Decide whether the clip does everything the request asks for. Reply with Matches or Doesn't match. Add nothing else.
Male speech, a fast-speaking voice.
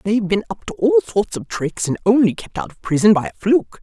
Doesn't match